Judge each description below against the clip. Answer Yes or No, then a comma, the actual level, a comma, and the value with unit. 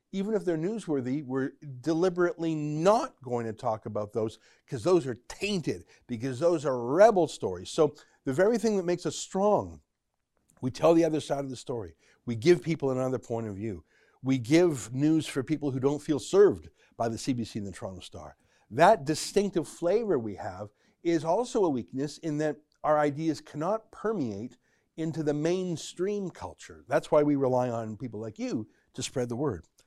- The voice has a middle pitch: Yes, medium, 150 Hz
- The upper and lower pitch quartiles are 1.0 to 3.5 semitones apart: No, wide, 5.6 semitones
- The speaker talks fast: No, average, 185 wpm